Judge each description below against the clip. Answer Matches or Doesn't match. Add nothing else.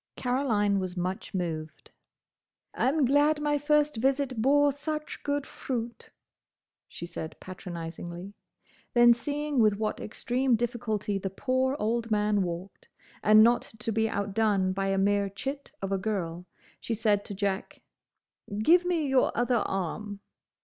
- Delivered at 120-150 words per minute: Matches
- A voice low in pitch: Doesn't match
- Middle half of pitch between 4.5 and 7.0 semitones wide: Matches